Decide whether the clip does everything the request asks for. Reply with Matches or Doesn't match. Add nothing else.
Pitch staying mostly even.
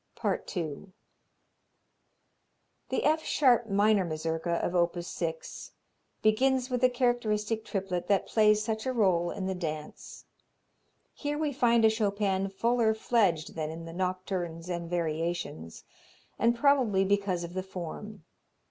Doesn't match